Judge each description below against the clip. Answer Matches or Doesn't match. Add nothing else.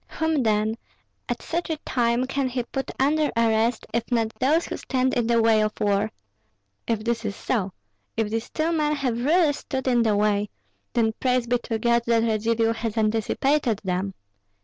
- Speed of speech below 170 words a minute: Doesn't match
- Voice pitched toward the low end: Doesn't match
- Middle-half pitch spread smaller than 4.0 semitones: Matches